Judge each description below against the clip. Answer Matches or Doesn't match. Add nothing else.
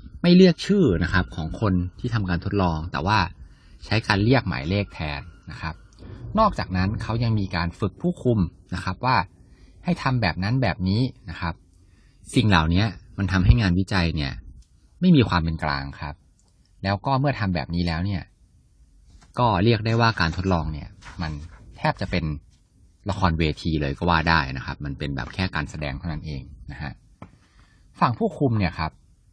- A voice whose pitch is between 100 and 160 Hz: Doesn't match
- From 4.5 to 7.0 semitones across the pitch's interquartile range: Matches